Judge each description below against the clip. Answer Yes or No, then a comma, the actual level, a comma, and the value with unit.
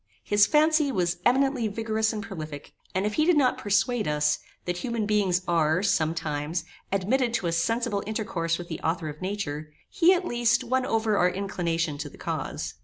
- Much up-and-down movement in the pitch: Yes, wide, 6.0 semitones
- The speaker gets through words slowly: No, average, 180 wpm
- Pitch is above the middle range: Yes, high, 200 Hz